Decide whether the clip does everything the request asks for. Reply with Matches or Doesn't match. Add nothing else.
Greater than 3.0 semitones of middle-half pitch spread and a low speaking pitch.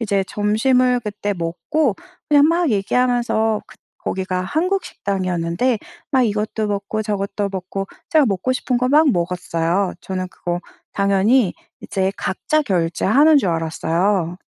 Doesn't match